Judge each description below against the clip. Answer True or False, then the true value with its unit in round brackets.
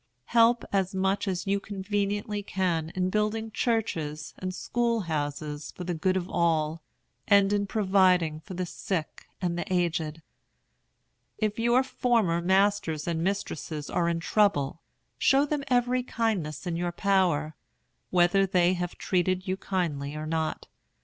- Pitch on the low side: False (185 Hz)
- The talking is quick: False (145 wpm)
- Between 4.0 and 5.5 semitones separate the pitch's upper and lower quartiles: False (3.6 semitones)